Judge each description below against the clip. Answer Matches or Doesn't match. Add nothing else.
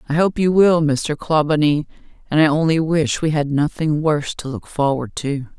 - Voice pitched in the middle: Matches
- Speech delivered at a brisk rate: Doesn't match